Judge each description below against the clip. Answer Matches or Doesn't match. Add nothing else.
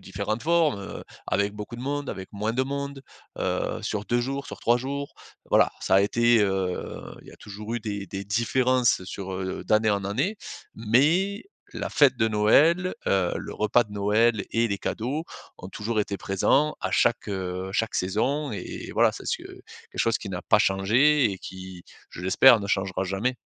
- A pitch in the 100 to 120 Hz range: Matches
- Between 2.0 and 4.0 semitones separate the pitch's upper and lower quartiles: Doesn't match